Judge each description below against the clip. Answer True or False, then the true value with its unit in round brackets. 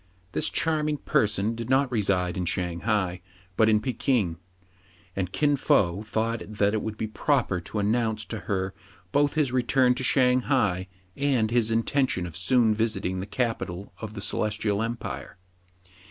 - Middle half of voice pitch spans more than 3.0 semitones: True (4.1 semitones)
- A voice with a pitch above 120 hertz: False (110 Hz)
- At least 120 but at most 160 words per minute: False (170 wpm)